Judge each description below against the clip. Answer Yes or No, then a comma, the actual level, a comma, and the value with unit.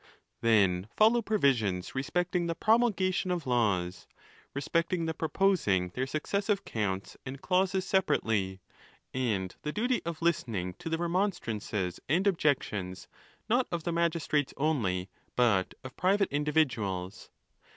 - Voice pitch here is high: No, medium, 150 Hz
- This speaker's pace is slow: Yes, slow, 125 wpm